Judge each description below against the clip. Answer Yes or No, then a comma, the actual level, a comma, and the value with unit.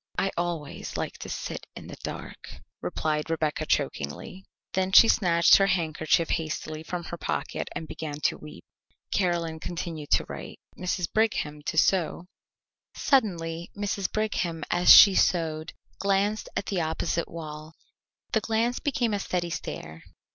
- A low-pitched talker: No, medium, 170 Hz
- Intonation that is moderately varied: Yes, average, 3.6 semitones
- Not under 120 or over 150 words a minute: Yes, average, 145 wpm